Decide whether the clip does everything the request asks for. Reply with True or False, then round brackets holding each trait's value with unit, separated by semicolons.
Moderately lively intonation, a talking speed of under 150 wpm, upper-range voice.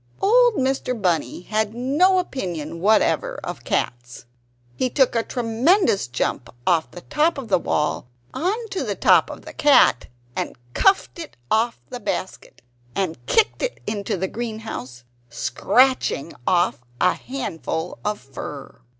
False (8.4 semitones; 140 wpm; 220 Hz)